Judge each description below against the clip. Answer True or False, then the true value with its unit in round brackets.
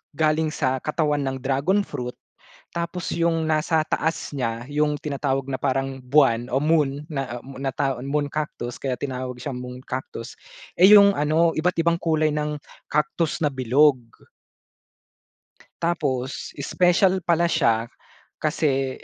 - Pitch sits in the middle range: True (145 Hz)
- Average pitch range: True (3.4 semitones)